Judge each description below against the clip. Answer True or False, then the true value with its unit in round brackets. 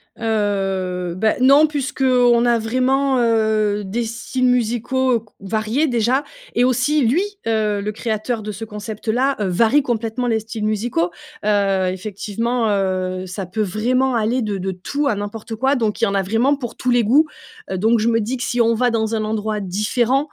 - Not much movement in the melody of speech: False (3.1 semitones)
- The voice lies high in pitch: True (225 Hz)